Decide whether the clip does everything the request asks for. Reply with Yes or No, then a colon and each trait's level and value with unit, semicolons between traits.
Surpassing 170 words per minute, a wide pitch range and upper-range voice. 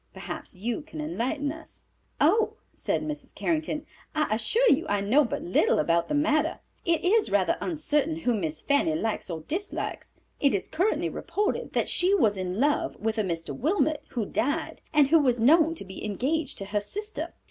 Yes: average, 185 wpm; wide, 7.0 semitones; very high, 290 Hz